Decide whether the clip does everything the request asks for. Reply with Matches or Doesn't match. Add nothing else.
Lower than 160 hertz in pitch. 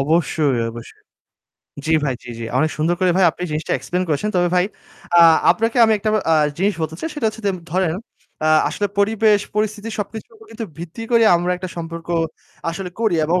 Doesn't match